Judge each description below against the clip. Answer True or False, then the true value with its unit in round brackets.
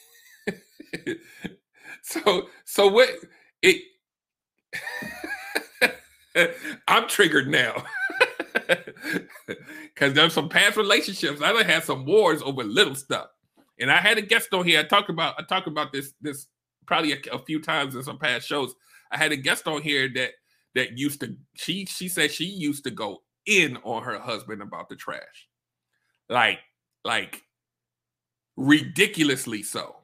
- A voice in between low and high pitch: True (170 Hz)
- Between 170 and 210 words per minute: False (140 wpm)